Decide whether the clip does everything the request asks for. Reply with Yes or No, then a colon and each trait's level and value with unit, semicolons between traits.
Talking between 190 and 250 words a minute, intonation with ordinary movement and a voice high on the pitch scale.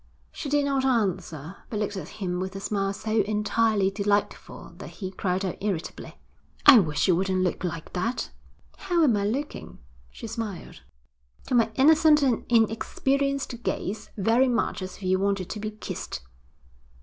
No: average, 165 wpm; average, 4.2 semitones; high, 210 Hz